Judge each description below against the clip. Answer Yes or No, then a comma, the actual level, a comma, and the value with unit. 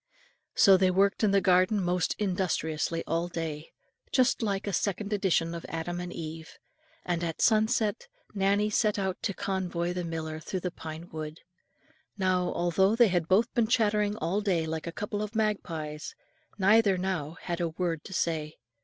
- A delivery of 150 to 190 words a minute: Yes, average, 170 wpm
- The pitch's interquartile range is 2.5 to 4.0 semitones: Yes, average, 3.6 semitones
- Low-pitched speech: No, medium, 185 Hz